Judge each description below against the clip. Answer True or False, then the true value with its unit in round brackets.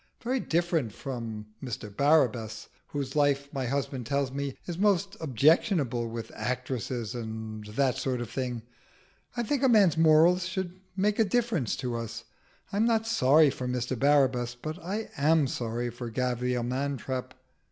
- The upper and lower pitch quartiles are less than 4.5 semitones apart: False (5.3 semitones)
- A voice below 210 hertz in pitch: True (135 Hz)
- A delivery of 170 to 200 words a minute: False (155 wpm)